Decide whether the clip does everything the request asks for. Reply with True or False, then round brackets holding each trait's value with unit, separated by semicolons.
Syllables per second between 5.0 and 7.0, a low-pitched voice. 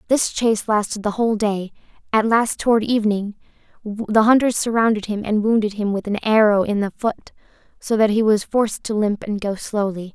False (5.4 syllables/s; 215 Hz)